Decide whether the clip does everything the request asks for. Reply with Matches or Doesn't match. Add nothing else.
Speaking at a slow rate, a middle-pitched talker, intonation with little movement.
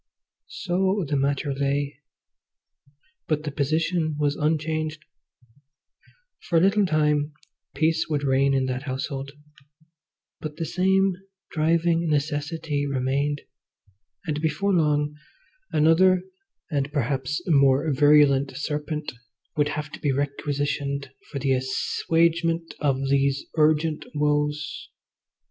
Matches